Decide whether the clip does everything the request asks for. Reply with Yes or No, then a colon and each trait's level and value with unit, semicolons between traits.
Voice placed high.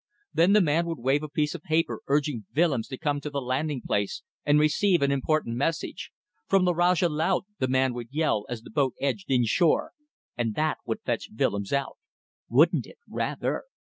No: medium, 145 Hz